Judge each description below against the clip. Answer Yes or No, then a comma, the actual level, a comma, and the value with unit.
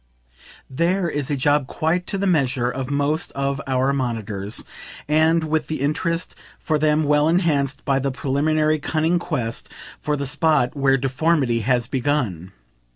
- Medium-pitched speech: Yes, medium, 145 Hz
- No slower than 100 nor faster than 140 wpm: No, average, 155 wpm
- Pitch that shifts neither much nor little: Yes, average, 3.0 semitones